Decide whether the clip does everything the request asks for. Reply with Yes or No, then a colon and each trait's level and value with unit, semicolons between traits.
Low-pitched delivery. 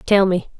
No: high, 190 Hz